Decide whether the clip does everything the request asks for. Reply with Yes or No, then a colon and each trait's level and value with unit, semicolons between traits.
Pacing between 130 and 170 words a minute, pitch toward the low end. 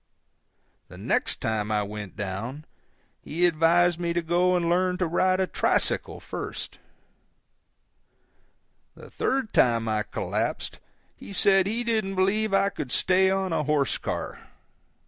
No: average, 140 wpm; medium, 175 Hz